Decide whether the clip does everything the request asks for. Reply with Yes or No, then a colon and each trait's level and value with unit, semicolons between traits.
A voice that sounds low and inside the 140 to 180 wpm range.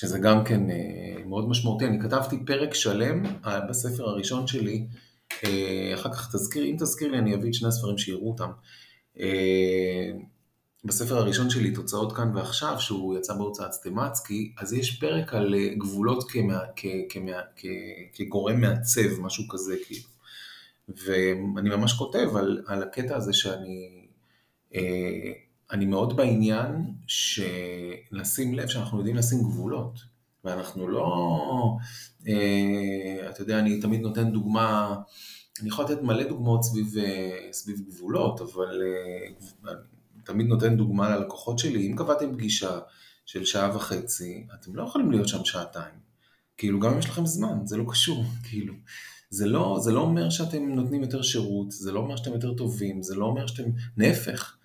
Yes: low, 110 Hz; average, 145 wpm